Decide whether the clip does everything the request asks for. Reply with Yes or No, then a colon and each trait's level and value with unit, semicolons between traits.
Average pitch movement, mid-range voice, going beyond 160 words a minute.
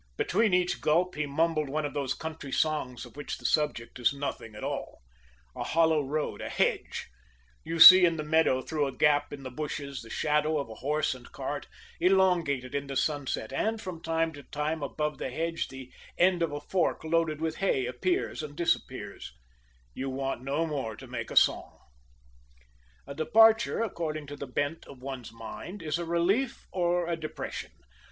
Yes: average, 3.3 semitones; medium, 150 Hz; average, 185 wpm